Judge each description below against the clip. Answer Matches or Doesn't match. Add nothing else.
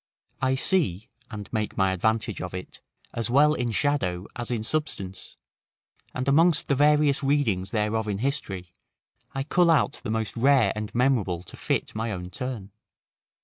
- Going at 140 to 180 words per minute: Matches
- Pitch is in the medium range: Doesn't match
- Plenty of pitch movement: Matches